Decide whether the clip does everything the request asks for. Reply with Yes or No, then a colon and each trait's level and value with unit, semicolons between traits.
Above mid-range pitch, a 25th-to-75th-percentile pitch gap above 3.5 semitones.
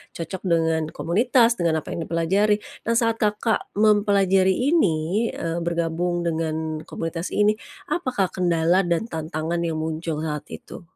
No: medium, 170 Hz; average, 4.2 semitones